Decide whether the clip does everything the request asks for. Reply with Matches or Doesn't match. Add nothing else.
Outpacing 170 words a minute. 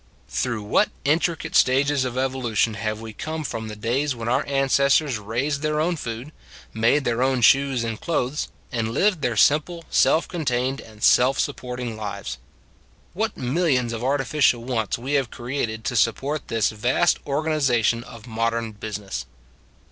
Doesn't match